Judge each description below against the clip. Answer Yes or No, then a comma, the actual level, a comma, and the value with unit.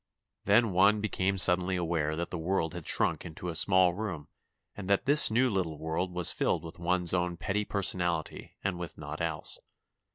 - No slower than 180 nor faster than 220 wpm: Yes, average, 185 wpm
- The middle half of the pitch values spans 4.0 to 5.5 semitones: No, average, 2.8 semitones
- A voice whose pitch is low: Yes, very low, 90 Hz